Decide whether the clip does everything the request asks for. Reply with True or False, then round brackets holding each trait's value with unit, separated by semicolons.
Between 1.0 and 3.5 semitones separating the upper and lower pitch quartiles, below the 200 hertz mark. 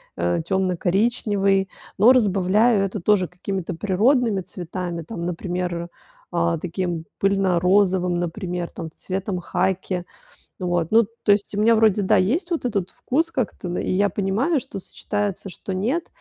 True (2.8 semitones; 190 Hz)